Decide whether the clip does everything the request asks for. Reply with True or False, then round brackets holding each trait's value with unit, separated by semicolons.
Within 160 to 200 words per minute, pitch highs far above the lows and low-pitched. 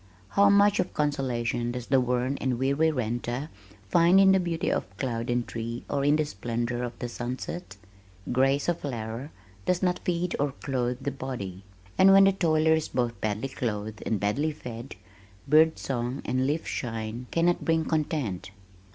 False (170 wpm; 5.0 semitones; 130 Hz)